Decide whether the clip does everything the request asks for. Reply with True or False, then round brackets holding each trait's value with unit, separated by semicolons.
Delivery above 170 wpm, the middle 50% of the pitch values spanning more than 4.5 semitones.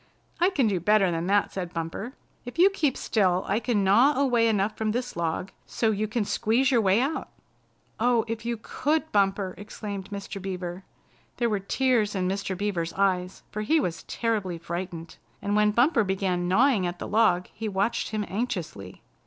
False (185 wpm; 3.9 semitones)